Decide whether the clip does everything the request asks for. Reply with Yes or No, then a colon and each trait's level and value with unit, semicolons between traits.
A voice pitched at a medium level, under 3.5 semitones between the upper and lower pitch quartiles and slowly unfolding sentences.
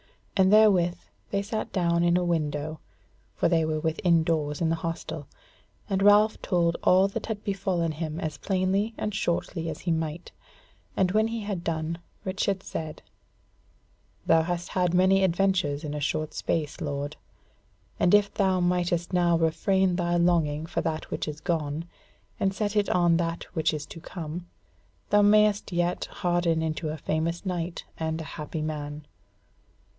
No: medium, 170 Hz; average, 3.1 semitones; average, 165 wpm